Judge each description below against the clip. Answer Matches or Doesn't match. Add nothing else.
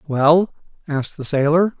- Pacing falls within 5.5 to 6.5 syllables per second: Doesn't match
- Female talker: Doesn't match